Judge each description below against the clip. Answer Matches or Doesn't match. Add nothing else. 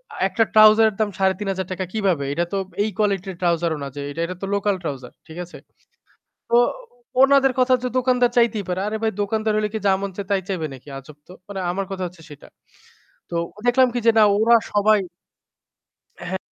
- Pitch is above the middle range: Matches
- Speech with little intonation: Doesn't match